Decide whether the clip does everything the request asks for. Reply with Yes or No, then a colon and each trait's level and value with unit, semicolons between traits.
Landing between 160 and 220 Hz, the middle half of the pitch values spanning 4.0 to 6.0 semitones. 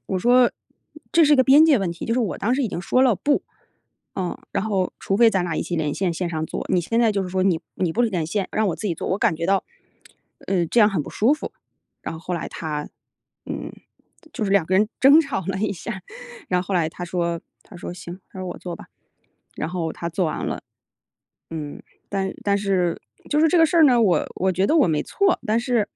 Yes: high, 190 Hz; average, 5.1 semitones